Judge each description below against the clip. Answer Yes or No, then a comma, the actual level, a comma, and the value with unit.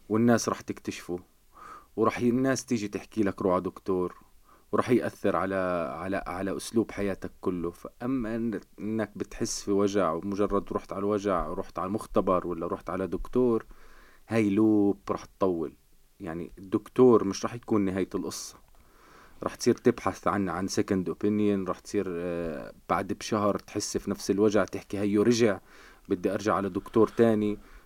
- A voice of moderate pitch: No, low, 100 Hz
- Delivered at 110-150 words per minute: Yes, average, 145 wpm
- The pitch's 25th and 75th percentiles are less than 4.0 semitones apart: Yes, average, 2.8 semitones